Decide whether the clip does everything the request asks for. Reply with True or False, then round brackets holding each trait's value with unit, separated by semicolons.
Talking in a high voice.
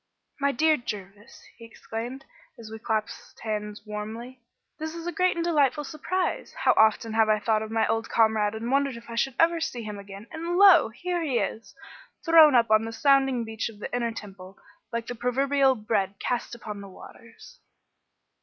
True (230 Hz)